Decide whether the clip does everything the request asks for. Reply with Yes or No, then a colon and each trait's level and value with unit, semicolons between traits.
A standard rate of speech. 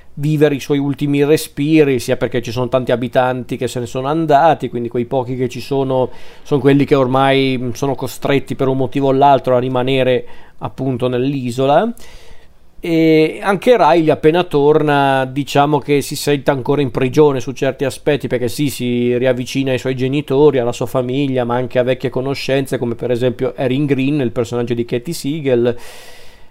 No: fast, 175 wpm